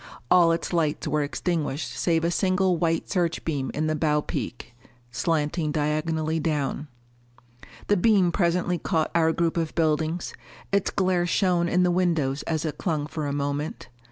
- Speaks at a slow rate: No, average, 160 wpm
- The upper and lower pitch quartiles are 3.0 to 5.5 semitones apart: No, narrow, 2.5 semitones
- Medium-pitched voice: Yes, medium, 165 Hz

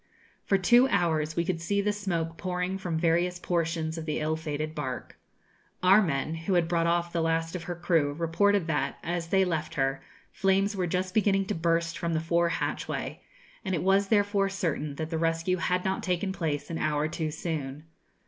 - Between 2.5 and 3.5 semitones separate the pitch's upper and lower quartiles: Yes, average, 2.8 semitones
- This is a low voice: No, medium, 170 Hz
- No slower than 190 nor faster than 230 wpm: Yes, average, 195 wpm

